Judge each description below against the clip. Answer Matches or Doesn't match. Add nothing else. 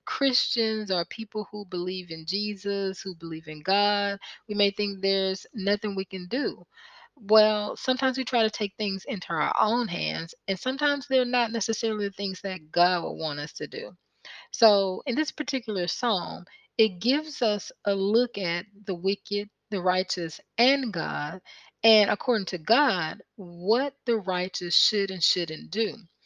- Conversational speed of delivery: Matches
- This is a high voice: Matches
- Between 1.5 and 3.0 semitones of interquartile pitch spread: Doesn't match